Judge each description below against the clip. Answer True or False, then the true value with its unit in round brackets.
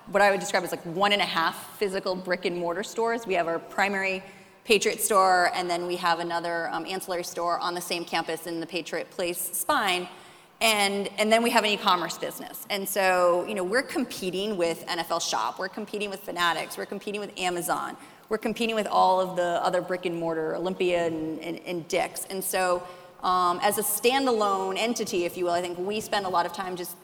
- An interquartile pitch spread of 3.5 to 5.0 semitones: False (2.7 semitones)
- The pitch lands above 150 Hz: True (185 Hz)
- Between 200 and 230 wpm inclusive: True (205 wpm)